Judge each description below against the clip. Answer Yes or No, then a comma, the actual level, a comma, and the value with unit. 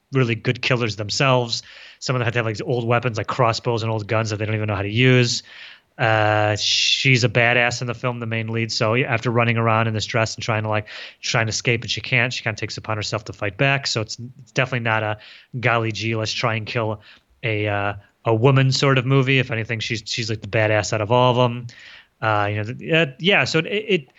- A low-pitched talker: Yes, low, 115 Hz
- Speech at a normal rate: No, fast, 255 wpm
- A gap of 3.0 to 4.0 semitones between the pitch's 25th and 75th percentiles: No, narrow, 2.4 semitones